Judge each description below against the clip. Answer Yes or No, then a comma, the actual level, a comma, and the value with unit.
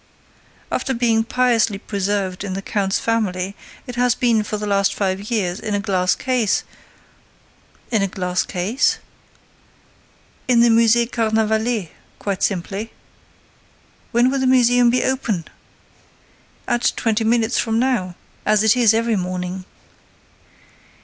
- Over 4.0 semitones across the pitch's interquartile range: No, average, 3.4 semitones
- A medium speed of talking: No, slow, 130 wpm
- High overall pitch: Yes, high, 220 Hz